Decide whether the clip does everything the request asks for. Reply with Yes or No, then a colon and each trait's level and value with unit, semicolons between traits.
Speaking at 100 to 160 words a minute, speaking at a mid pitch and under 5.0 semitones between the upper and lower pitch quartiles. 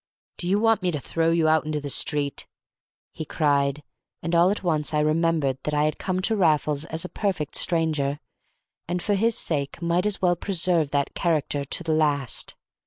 No: average, 195 wpm; medium, 160 Hz; average, 3.2 semitones